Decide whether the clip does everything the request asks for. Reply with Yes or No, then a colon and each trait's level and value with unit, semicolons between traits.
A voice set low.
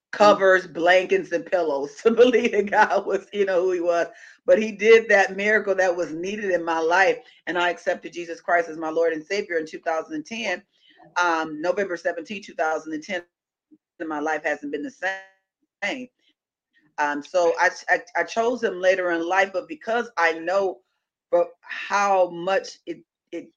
No: medium, 185 Hz